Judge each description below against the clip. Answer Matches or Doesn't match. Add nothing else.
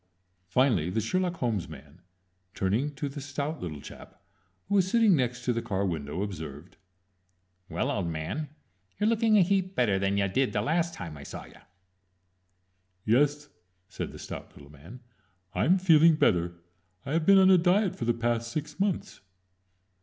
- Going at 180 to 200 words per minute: Doesn't match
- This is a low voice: Matches